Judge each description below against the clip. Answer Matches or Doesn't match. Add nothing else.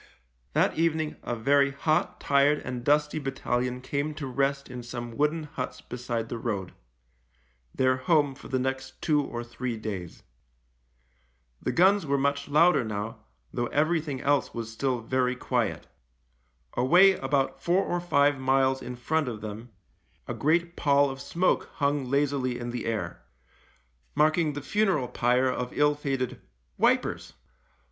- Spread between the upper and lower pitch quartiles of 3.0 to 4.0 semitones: Matches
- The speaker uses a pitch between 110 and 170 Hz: Matches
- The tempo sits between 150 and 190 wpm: Matches